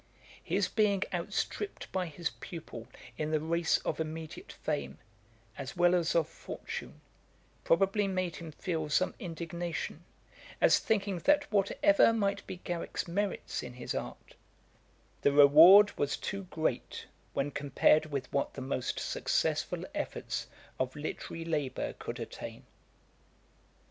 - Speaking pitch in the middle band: Yes, medium, 170 Hz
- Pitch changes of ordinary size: Yes, average, 4.3 semitones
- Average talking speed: No, slow, 130 wpm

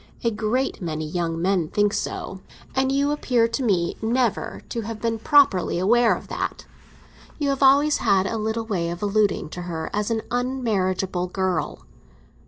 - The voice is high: Yes, high, 215 Hz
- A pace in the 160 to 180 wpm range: Yes, average, 170 wpm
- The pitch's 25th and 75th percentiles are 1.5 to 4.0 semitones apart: No, average, 4.8 semitones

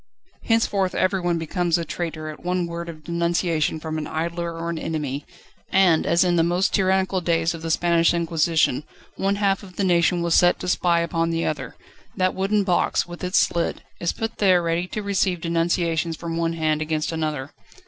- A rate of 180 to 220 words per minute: Yes, average, 190 wpm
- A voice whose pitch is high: No, medium, 170 Hz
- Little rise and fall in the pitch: Yes, narrow, 1.8 semitones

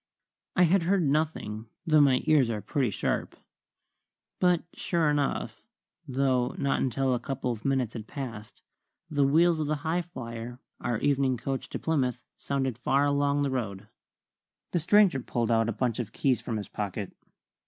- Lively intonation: No, average, 4.1 semitones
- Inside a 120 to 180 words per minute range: Yes, average, 165 wpm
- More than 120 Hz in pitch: Yes, low, 135 Hz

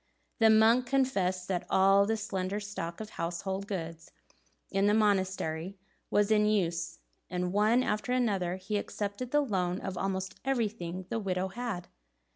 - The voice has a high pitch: Yes, high, 195 Hz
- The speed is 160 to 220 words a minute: No, average, 150 wpm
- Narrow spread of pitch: No, average, 3.0 semitones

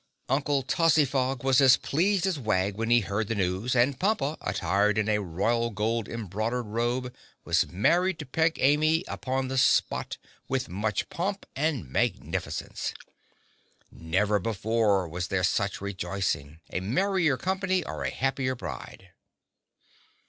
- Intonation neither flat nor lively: No, wide, 6.0 semitones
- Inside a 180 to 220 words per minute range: No, slow, 135 wpm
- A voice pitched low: Yes, low, 120 Hz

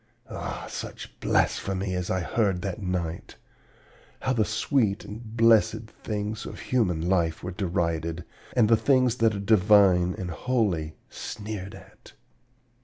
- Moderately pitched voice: No, low, 100 Hz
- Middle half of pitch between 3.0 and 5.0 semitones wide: Yes, average, 3.7 semitones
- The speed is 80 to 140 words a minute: Yes, slow, 135 wpm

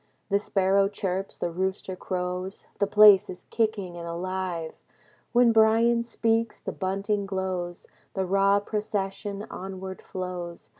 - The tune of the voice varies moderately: No, narrow, 2.2 semitones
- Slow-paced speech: Yes, slow, 130 wpm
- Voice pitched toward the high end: Yes, high, 195 Hz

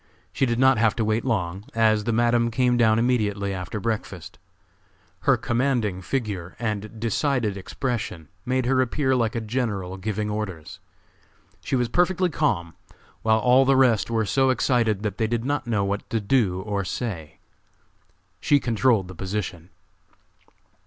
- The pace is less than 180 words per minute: Yes, average, 155 wpm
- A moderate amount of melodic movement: Yes, average, 3.8 semitones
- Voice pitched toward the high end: No, low, 110 Hz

